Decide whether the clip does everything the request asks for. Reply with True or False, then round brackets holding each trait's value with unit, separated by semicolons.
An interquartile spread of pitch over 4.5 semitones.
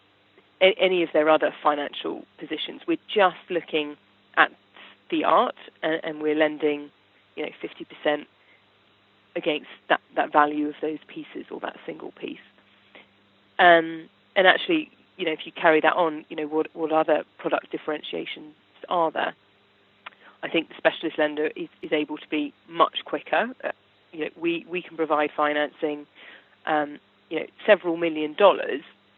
False (3.4 semitones)